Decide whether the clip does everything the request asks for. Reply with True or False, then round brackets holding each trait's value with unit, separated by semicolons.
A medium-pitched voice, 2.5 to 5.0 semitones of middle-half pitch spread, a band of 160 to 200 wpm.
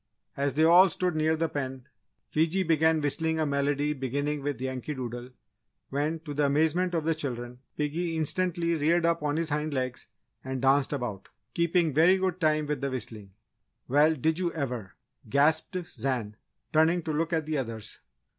True (150 Hz; 3.3 semitones; 175 wpm)